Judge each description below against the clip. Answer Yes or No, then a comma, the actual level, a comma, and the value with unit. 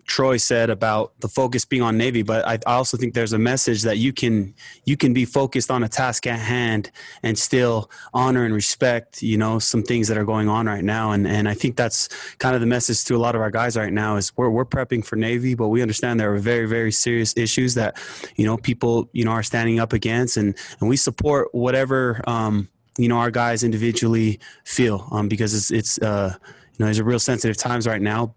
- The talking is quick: Yes, fast, 235 wpm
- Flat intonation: Yes, narrow, 2.1 semitones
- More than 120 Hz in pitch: No, low, 115 Hz